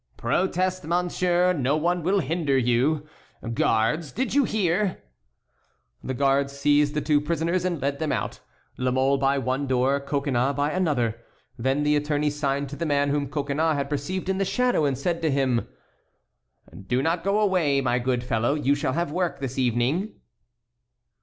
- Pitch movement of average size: Yes, average, 4.1 semitones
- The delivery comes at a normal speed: Yes, average, 170 wpm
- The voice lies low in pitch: No, medium, 145 Hz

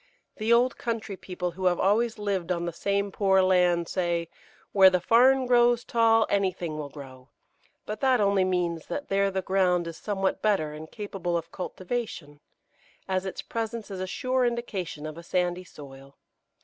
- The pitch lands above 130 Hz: Yes, high, 190 Hz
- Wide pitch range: No, average, 4.1 semitones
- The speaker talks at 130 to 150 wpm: No, average, 175 wpm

